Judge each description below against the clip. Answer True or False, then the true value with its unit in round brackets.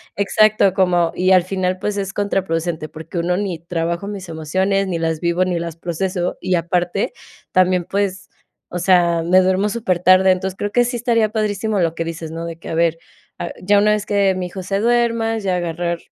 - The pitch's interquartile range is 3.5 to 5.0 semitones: False (2.8 semitones)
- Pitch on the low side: False (185 Hz)